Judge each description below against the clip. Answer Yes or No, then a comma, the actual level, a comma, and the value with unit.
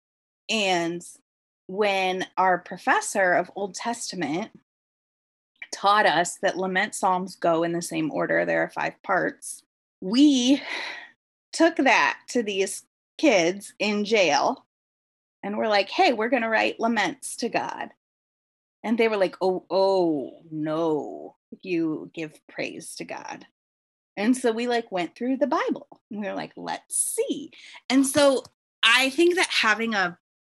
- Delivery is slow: No, average, 145 wpm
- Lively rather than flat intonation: Yes, wide, 6.1 semitones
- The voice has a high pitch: Yes, high, 205 Hz